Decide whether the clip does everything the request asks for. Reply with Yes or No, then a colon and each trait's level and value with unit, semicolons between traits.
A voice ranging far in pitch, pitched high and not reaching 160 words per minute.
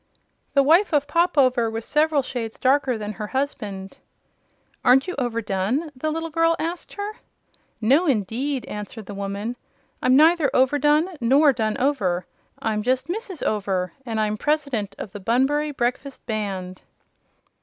Yes: wide, 5.8 semitones; very high, 255 Hz; average, 150 wpm